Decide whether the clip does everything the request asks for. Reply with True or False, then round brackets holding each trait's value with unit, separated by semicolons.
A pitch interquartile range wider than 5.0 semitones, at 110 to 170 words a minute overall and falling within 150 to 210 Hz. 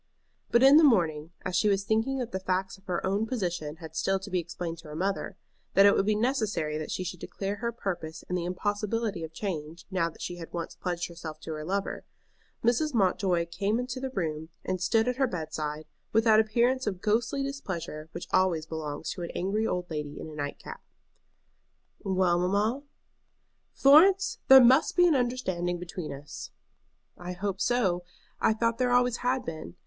False (5.4 semitones; 195 wpm; 190 Hz)